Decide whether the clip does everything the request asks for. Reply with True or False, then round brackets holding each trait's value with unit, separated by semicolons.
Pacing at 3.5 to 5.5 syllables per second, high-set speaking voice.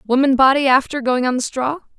False (6.1 syllables/s; 265 Hz)